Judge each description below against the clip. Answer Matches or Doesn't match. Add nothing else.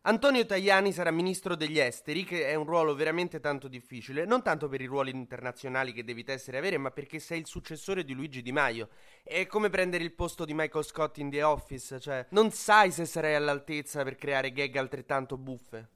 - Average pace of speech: Doesn't match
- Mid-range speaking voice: Matches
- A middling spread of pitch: Matches